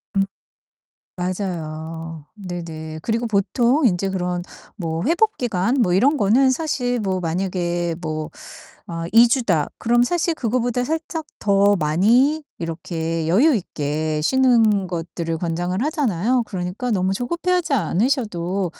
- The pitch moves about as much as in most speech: No, wide, 6.5 semitones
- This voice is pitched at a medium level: No, high, 195 Hz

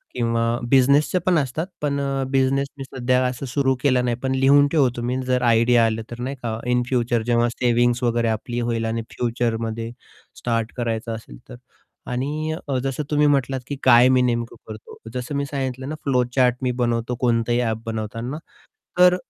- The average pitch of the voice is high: No, low, 125 Hz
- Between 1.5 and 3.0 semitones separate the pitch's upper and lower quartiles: Yes, narrow, 2.6 semitones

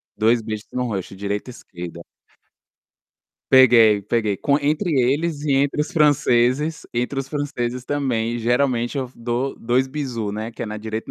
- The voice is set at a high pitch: No, low, 120 Hz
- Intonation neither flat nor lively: Yes, average, 3.7 semitones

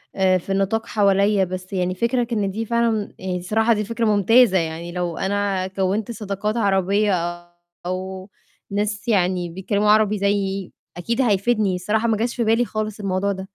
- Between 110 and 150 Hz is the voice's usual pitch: No, high, 200 Hz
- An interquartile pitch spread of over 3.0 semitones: No, narrow, 2.5 semitones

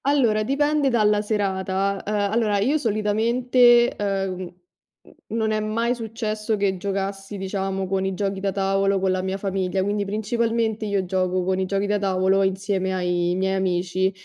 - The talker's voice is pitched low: No, high, 200 Hz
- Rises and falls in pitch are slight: Yes, narrow, 2.2 semitones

